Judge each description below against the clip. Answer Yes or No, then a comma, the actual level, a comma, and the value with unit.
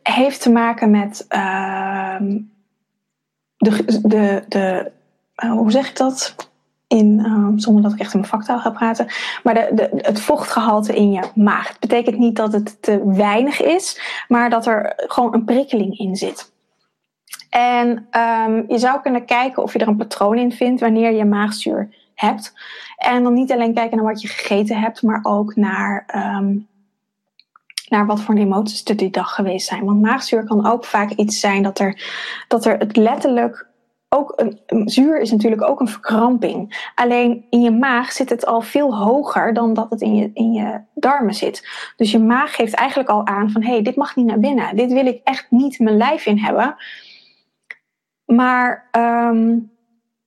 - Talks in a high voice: Yes, high, 225 Hz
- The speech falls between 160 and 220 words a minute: Yes, average, 185 wpm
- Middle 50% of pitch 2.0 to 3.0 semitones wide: Yes, narrow, 2.6 semitones